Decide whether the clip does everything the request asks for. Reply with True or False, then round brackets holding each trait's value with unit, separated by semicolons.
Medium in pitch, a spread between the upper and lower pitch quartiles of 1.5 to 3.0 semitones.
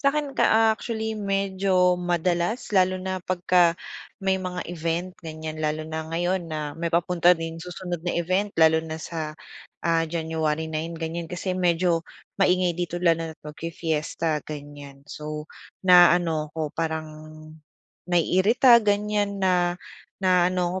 True (175 Hz; 2.5 semitones)